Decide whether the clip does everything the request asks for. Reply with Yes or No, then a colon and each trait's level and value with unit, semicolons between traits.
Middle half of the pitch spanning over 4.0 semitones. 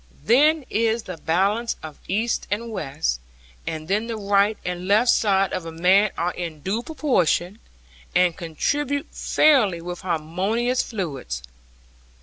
Yes: average, 5.1 semitones